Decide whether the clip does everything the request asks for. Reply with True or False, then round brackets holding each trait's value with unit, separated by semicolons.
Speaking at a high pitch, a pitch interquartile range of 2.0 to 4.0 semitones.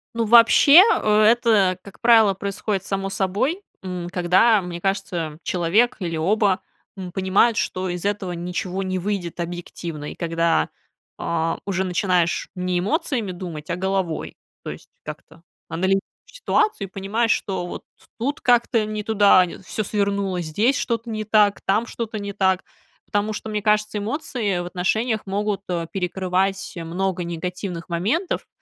True (195 Hz; 3.2 semitones)